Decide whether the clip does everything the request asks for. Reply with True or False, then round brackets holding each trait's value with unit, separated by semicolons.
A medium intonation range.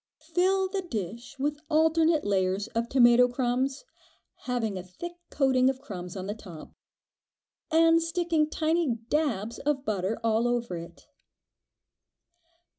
False (6.6 semitones)